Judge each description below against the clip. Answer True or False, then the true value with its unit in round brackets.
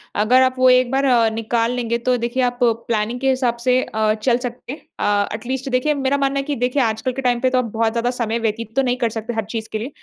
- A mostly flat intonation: True (2.2 semitones)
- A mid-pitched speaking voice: False (245 Hz)